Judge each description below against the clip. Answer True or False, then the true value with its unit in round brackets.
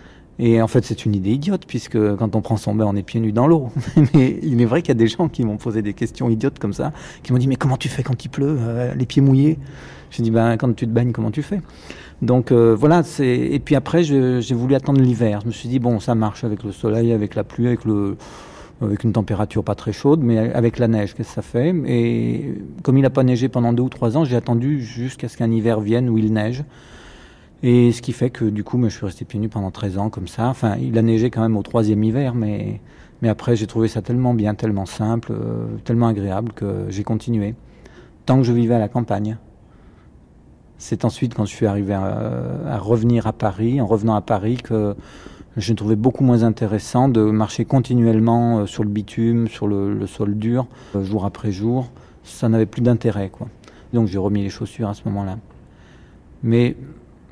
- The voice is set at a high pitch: False (115 Hz)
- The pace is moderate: False (230 wpm)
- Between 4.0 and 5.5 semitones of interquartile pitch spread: False (2.7 semitones)